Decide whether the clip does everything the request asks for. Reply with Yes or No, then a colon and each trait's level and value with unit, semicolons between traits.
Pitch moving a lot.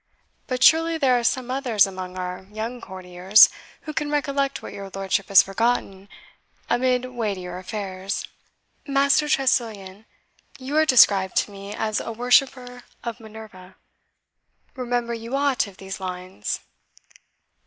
No: average, 4.9 semitones